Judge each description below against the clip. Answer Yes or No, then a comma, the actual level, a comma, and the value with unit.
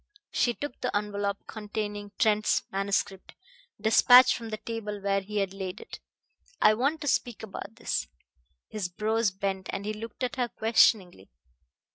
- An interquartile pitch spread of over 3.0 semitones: No, narrow, 2.4 semitones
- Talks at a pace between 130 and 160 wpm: Yes, average, 155 wpm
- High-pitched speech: Yes, high, 210 Hz